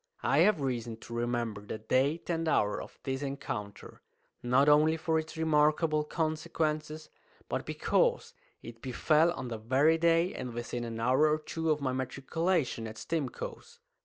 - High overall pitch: No, medium, 150 Hz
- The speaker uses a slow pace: No, average, 160 wpm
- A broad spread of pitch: No, average, 4.8 semitones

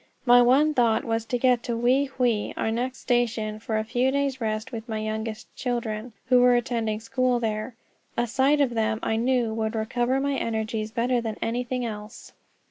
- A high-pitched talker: Yes, high, 235 Hz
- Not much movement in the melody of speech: Yes, narrow, 2.3 semitones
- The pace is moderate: Yes, average, 190 wpm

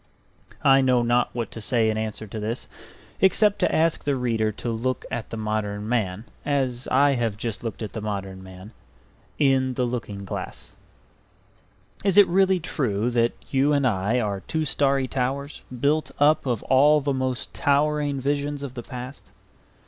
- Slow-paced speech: No, average, 170 wpm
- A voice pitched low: Yes, low, 125 Hz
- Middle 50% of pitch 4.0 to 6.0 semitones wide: Yes, average, 4.4 semitones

